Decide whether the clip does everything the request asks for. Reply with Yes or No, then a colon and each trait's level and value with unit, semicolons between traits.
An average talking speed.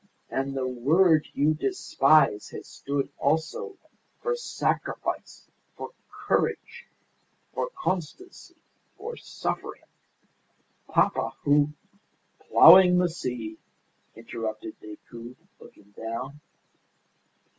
No: slow, 90 wpm